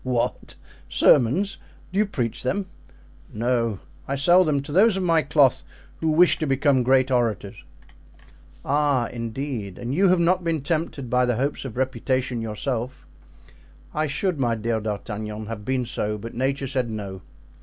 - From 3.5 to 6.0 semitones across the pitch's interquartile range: Yes, average, 4.5 semitones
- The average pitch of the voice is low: Yes, low, 130 Hz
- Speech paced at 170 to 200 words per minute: No, average, 160 wpm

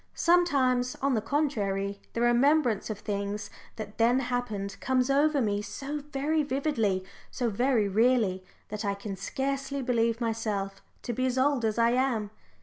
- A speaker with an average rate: Yes, average, 160 wpm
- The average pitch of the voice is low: No, high, 240 Hz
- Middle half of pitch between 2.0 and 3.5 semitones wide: No, average, 4.6 semitones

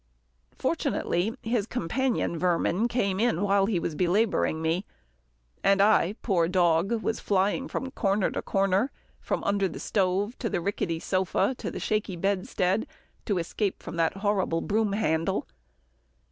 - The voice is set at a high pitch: Yes, high, 195 Hz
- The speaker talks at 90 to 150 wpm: Yes, average, 145 wpm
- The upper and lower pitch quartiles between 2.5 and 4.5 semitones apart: Yes, average, 3.3 semitones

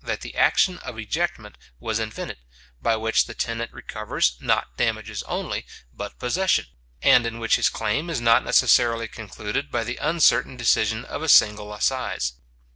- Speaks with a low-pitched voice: Yes, low, 115 Hz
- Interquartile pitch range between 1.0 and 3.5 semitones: Yes, average, 2.8 semitones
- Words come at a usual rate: Yes, average, 160 wpm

